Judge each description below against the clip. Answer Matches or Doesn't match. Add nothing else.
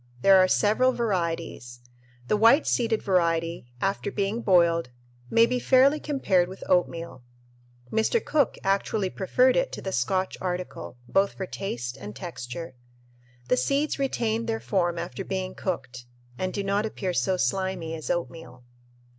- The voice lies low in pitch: Doesn't match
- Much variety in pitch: Doesn't match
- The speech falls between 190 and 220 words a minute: Doesn't match